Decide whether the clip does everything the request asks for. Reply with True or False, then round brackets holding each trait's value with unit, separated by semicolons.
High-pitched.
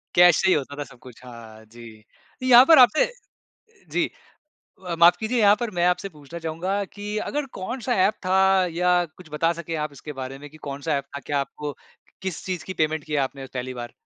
False (165 Hz)